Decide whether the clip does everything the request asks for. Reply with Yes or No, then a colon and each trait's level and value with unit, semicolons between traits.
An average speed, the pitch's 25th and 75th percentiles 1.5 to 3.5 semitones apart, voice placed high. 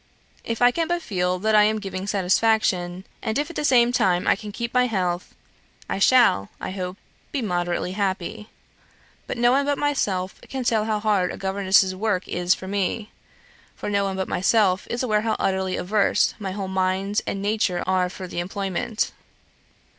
Yes: average, 185 wpm; average, 3.1 semitones; high, 200 Hz